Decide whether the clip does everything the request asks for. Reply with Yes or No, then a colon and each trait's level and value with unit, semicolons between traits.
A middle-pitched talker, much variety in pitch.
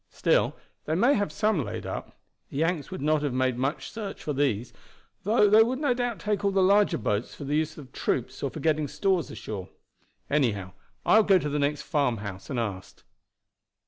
Yes: medium, 150 Hz; wide, 7.7 semitones